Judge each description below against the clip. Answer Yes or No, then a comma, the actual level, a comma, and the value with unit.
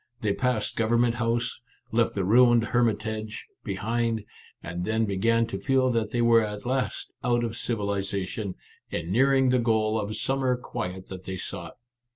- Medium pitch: No, low, 115 Hz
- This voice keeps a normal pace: Yes, average, 165 wpm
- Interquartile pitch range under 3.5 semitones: Yes, average, 2.7 semitones